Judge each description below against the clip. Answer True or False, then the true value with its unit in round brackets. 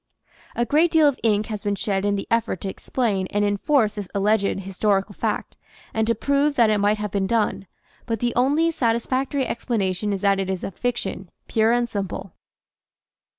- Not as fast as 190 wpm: False (195 wpm)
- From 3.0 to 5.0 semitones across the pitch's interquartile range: True (3.4 semitones)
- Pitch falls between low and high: False (215 Hz)